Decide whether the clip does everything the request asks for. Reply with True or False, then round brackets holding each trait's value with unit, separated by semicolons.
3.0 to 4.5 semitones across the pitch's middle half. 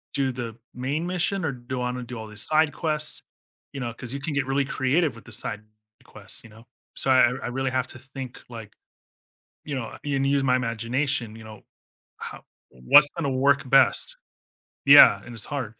True (3.3 semitones)